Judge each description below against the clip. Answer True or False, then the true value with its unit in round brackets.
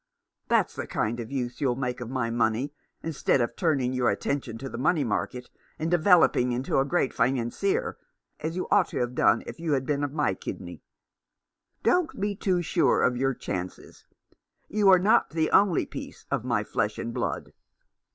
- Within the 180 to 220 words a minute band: True (185 wpm)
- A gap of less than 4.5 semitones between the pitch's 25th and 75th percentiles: False (5.6 semitones)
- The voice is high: False (135 Hz)